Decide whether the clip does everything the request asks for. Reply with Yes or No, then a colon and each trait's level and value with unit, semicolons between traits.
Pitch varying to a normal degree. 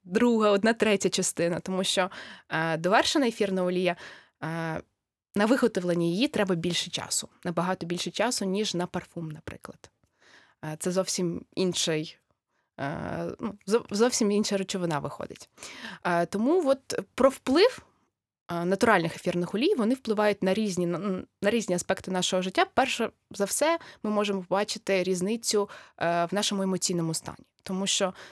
Yes: average, 3.3 semitones